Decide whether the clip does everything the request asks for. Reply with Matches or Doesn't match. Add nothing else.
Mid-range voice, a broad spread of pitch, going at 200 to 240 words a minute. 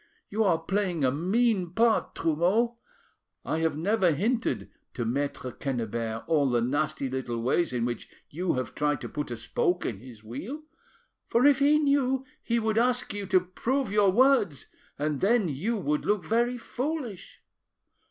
Doesn't match